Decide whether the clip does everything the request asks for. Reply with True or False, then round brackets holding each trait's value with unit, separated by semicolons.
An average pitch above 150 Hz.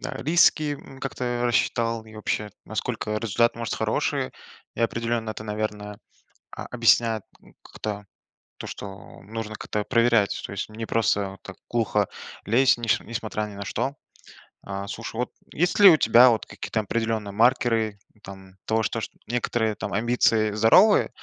False (115 Hz)